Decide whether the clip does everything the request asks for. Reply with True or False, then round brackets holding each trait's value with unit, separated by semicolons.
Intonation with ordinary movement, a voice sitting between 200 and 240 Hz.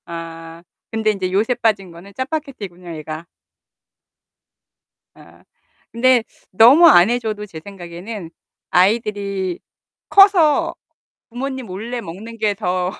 True (4.9 semitones; 205 Hz)